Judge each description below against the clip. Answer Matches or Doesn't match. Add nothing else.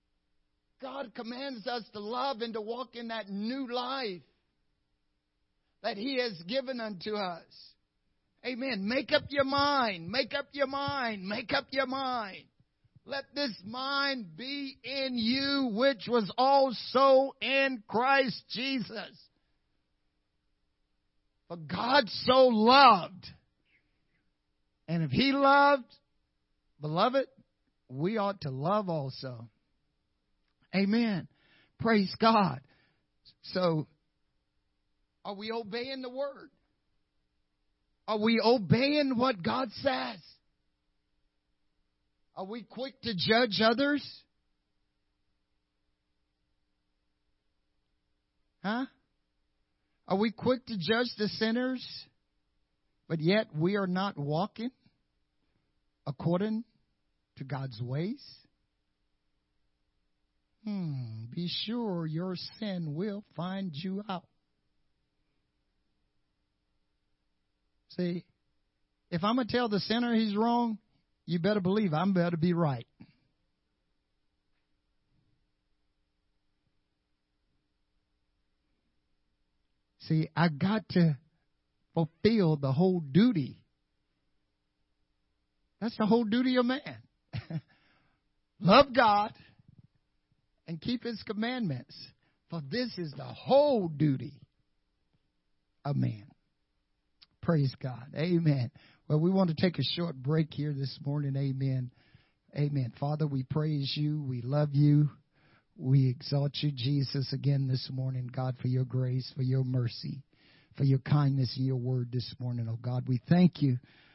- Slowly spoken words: Matches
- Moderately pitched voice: Matches